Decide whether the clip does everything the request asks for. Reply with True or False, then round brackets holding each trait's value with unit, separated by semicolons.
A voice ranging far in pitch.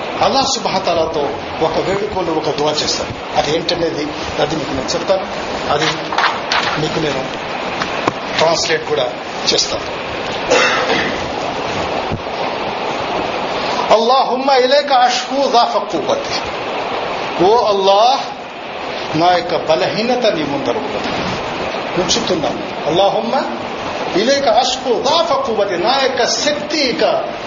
True (8.4 semitones)